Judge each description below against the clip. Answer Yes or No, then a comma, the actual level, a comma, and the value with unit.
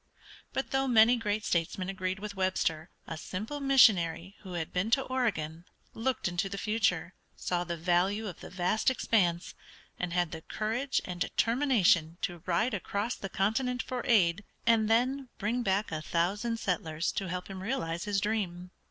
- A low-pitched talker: No, high, 195 Hz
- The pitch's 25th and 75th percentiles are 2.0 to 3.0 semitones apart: No, average, 4.5 semitones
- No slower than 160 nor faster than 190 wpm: Yes, average, 170 wpm